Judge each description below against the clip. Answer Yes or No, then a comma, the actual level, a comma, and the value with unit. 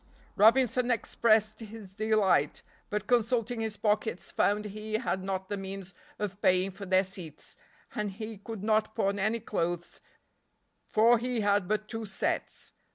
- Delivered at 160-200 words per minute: No, average, 150 wpm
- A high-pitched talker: Yes, high, 210 Hz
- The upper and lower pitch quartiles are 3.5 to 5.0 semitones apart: No, narrow, 2.4 semitones